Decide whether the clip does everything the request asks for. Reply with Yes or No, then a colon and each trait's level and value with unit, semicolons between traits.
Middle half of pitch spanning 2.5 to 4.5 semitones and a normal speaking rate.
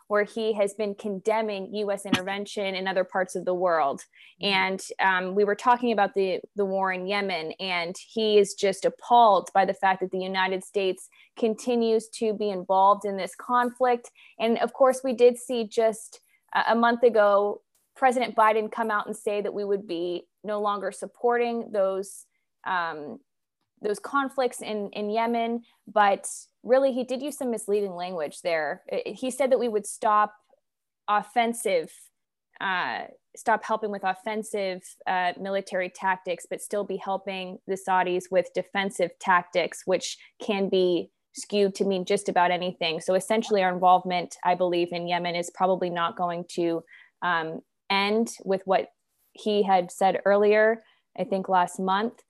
Yes: average, 3.1 semitones; average, 160 wpm